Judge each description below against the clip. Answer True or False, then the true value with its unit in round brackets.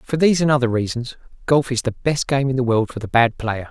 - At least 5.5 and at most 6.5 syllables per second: True (6.0 syllables/s)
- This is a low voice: True (125 Hz)